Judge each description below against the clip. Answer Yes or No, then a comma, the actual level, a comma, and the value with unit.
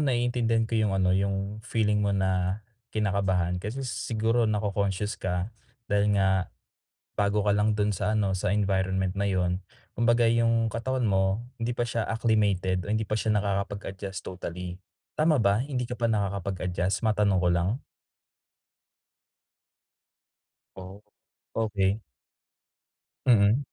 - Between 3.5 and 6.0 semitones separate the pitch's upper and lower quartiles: No, average, 2.8 semitones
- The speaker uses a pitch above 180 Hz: No, low, 100 Hz